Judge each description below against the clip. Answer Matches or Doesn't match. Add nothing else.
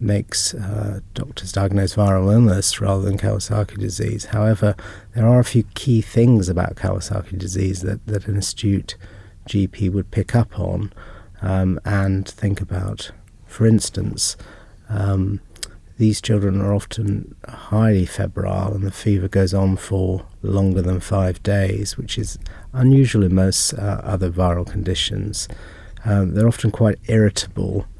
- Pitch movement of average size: Doesn't match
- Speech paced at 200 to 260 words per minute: Doesn't match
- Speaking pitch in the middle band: Doesn't match